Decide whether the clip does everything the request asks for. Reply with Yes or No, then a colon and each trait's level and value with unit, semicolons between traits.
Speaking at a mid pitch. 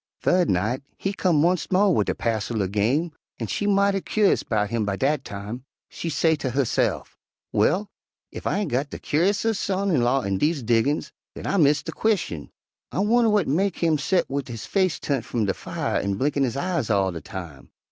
Yes: medium, 145 Hz